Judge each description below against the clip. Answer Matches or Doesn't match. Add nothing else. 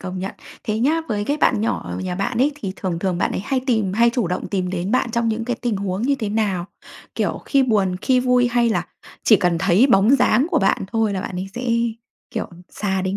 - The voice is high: Matches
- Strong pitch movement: Doesn't match